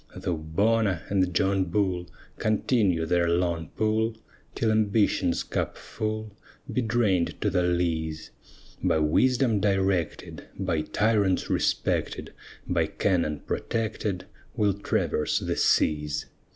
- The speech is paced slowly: Yes, slow, 110 wpm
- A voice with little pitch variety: No, average, 4.2 semitones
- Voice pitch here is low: Yes, very low, 95 Hz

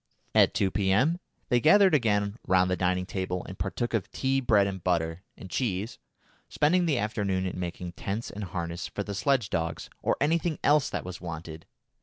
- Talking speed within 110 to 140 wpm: No, average, 185 wpm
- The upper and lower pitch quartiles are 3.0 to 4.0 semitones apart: No, average, 5.2 semitones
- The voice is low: Yes, low, 100 Hz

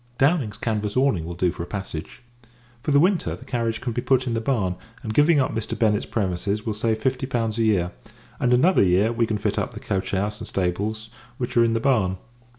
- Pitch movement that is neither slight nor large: Yes, average, 3.7 semitones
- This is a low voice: Yes, low, 110 Hz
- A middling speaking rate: No, fast, 230 wpm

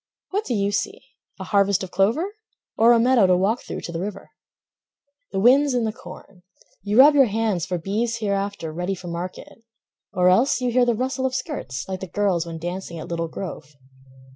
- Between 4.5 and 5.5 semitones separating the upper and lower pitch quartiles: Yes, average, 5.0 semitones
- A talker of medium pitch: No, high, 200 Hz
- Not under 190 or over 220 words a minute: Yes, average, 200 wpm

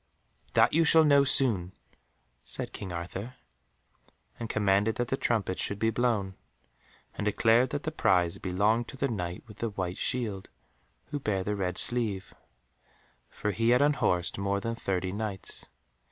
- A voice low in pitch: Yes, low, 105 Hz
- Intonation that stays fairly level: No, average, 4.1 semitones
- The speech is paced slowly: No, average, 155 wpm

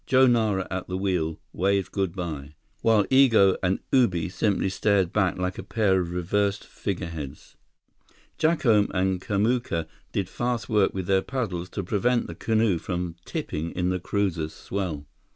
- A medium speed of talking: Yes, average, 155 wpm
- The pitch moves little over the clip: No, average, 3.2 semitones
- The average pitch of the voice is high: No, very low, 95 Hz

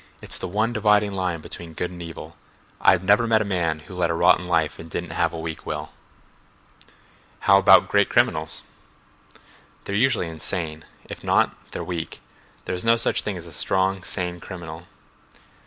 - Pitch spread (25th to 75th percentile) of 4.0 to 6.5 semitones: No, average, 3.1 semitones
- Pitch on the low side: Yes, very low, 90 Hz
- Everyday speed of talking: Yes, average, 175 wpm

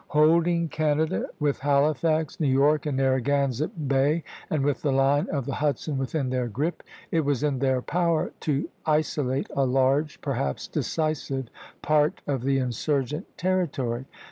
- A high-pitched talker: No, medium, 145 Hz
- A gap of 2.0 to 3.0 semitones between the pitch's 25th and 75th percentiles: Yes, narrow, 2.5 semitones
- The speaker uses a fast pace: No, average, 145 wpm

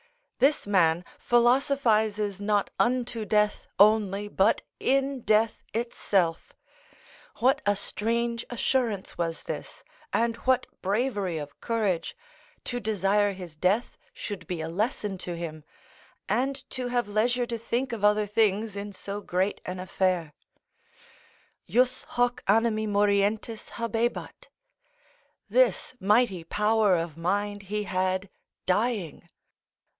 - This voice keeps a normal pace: No, slow, 120 wpm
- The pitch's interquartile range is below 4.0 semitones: Yes, average, 3.6 semitones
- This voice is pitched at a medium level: No, high, 210 Hz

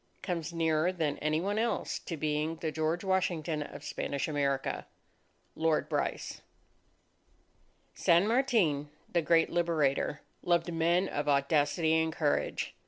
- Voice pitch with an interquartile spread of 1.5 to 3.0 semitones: Yes, narrow, 2.4 semitones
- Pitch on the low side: No, medium, 160 Hz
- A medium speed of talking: No, slow, 125 wpm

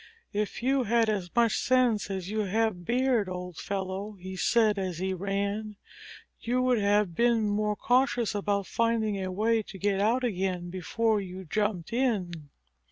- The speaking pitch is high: Yes, high, 205 Hz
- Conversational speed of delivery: Yes, average, 165 wpm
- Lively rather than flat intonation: No, average, 3.3 semitones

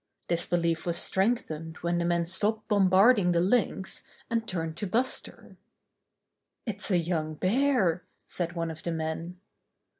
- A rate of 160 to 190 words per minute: No, average, 145 wpm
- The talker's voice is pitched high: No, medium, 175 Hz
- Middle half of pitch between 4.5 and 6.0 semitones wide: No, average, 3.6 semitones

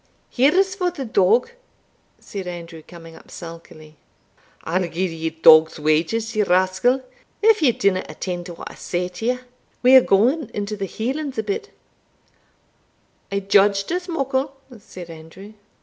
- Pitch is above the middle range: Yes, high, 200 Hz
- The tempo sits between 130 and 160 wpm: Yes, average, 150 wpm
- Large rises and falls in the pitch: Yes, wide, 6.9 semitones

